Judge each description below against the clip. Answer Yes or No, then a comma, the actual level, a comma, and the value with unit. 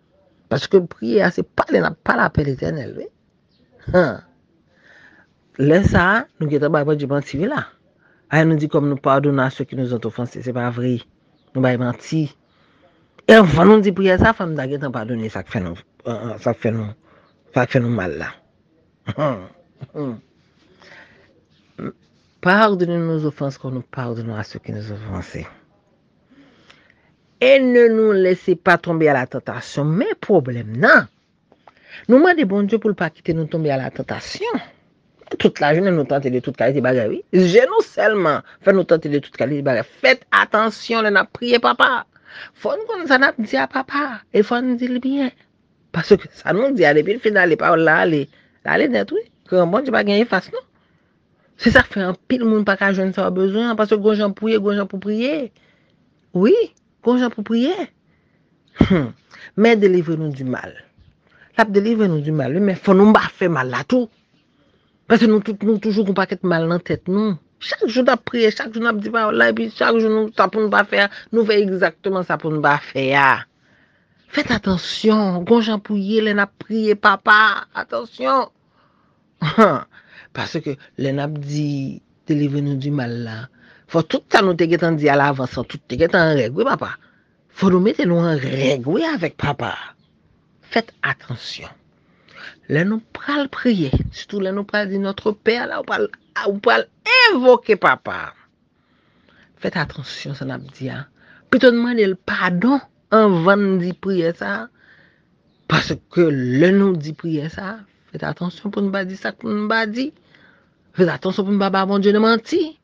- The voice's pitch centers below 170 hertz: No, medium, 185 Hz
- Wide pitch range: Yes, wide, 7.2 semitones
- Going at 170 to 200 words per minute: Yes, average, 185 wpm